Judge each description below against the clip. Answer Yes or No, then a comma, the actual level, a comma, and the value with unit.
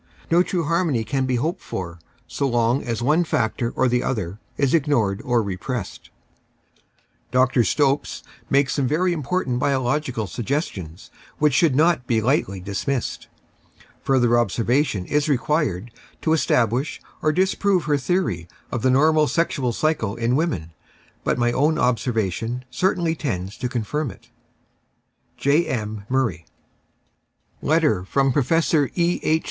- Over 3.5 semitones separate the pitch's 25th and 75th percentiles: Yes, average, 4.9 semitones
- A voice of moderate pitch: No, low, 130 Hz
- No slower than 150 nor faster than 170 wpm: No, average, 140 wpm